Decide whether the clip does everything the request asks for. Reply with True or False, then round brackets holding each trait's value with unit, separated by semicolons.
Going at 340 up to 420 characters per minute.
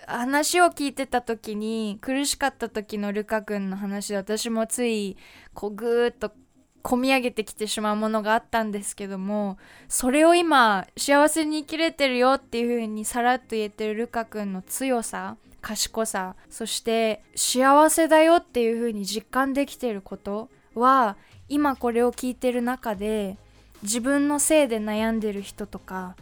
False (305 characters per minute)